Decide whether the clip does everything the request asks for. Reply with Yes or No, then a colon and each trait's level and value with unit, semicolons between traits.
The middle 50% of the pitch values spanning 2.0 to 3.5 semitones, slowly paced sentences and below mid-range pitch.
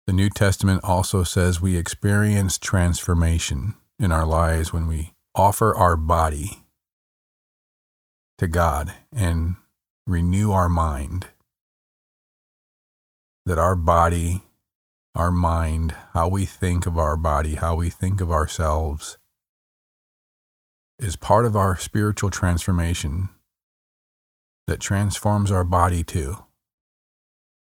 Yes: average, 2.9 semitones; slow, 105 wpm; very low, 90 Hz